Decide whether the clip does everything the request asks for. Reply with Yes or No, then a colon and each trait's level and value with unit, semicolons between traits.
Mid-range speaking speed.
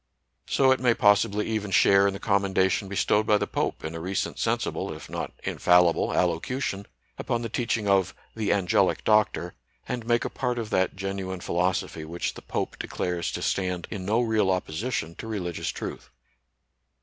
Yes: average, 175 wpm